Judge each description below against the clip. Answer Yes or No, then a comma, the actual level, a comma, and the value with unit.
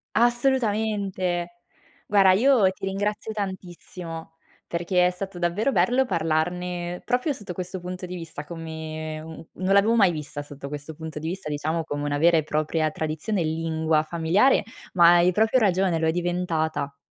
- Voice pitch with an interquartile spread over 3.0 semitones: Yes, average, 3.5 semitones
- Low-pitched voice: No, medium, 175 Hz